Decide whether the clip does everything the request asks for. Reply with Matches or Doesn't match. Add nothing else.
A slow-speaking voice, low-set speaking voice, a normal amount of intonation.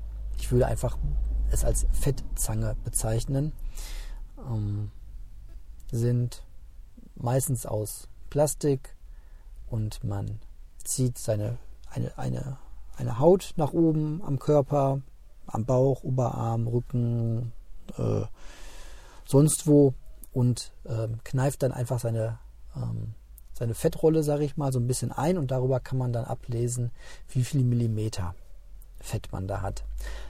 Matches